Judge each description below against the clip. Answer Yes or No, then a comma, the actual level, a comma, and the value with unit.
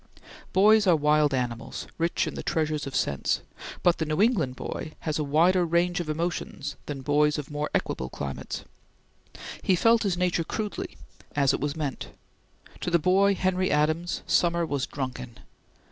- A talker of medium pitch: Yes, medium, 155 Hz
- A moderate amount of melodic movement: Yes, average, 3.6 semitones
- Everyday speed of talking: Yes, average, 165 wpm